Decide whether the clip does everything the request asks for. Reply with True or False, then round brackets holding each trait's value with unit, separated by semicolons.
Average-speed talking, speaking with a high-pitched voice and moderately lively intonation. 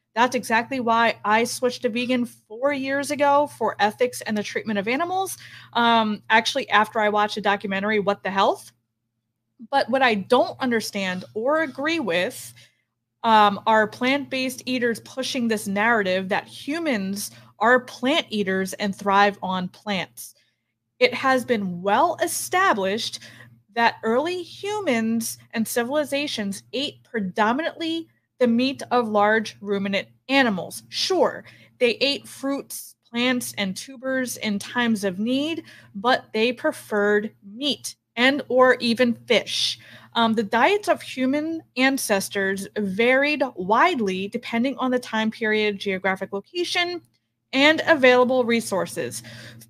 False (130 wpm; 230 Hz; 4.6 semitones)